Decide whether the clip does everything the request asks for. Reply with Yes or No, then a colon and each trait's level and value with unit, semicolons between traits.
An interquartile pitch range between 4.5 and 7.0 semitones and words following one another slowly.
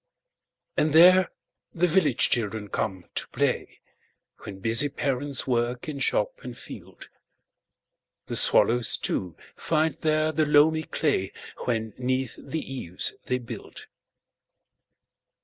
Yes: average, 5.2 semitones; slow, 105 wpm